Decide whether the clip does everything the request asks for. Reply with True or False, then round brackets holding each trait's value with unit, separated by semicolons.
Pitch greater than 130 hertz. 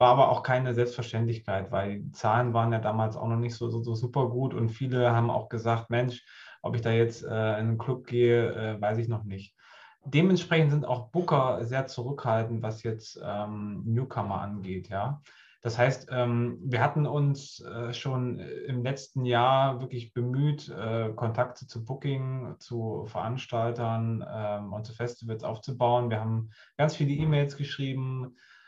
False (120 Hz)